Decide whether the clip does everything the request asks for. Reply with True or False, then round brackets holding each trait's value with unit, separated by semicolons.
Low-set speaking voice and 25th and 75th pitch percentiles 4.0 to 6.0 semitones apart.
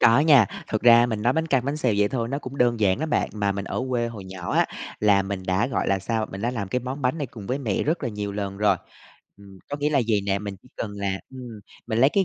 True (115 Hz; 4.4 semitones)